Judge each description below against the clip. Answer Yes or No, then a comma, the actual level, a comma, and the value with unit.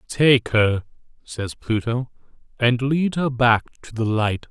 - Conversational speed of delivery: Yes, average, 145 wpm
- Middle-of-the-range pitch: No, low, 120 Hz